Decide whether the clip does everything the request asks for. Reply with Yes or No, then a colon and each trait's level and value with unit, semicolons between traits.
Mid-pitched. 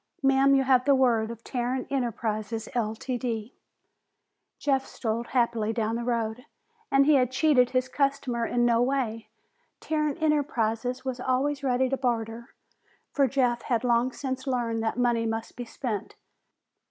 No: high, 245 Hz